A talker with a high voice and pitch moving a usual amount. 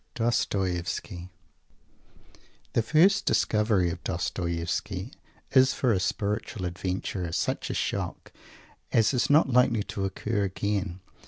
No: low, 100 Hz; average, 4.3 semitones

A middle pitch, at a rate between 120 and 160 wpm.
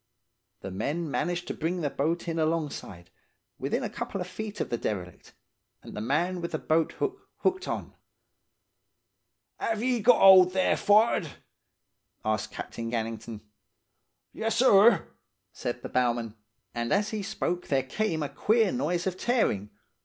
Yes: medium, 170 Hz; average, 150 wpm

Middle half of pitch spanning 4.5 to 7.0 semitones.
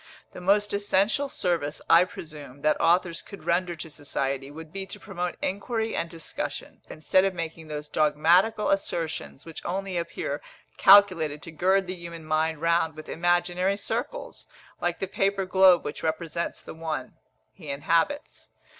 No: average, 3.4 semitones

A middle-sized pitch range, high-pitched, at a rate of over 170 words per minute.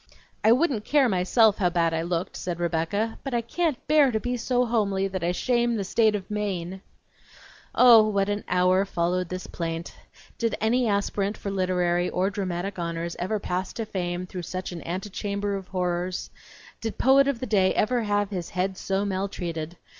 Yes: average, 3.6 semitones; high, 195 Hz; average, 185 wpm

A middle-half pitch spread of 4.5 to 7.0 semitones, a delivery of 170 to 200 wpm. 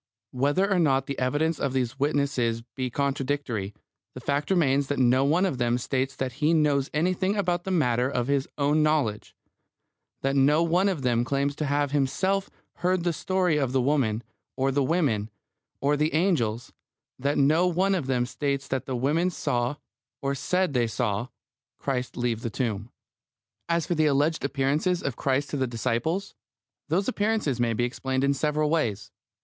No: average, 3.9 semitones; average, 175 wpm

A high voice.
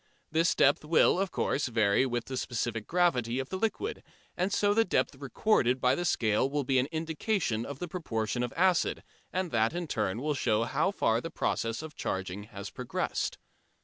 No: low, 135 Hz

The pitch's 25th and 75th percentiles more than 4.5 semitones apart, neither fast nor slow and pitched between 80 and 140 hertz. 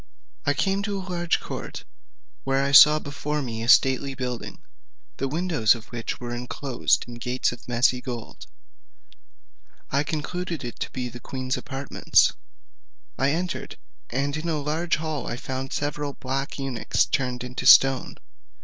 No: average, 3.3 semitones; average, 155 wpm; low, 135 Hz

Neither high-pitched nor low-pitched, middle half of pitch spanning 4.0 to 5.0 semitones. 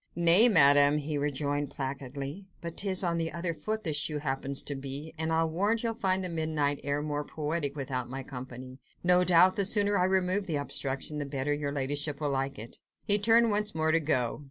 Yes: medium, 150 Hz; average, 4.3 semitones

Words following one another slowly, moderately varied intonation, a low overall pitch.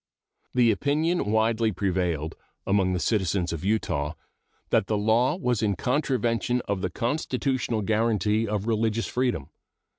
Yes: slow, 130 wpm; average, 3.7 semitones; low, 110 Hz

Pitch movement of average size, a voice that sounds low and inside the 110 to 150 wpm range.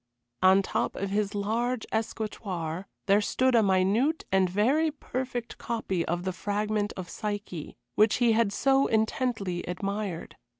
No: average, 3.4 semitones; high, 210 Hz; average, 140 wpm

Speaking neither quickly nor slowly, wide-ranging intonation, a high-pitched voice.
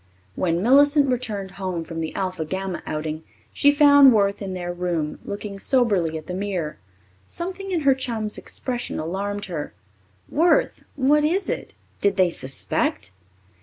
Yes: average, 150 wpm; wide, 7.3 semitones; high, 200 Hz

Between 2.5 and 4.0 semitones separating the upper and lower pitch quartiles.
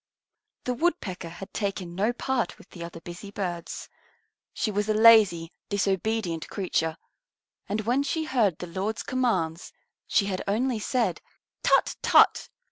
No: average, 4.6 semitones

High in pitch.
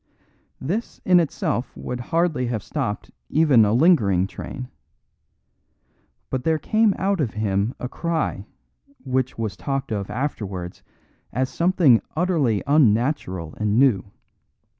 No: low, 130 Hz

